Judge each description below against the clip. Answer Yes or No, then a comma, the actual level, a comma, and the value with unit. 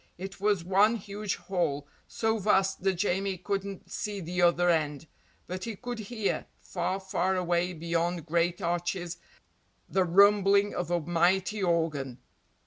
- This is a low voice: No, medium, 185 Hz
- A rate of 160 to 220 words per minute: No, average, 140 wpm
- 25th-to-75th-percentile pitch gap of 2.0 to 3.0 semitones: Yes, narrow, 2.5 semitones